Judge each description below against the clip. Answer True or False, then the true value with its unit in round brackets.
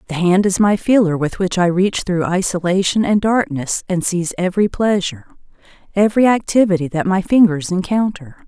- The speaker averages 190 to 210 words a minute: False (165 wpm)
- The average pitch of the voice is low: False (185 Hz)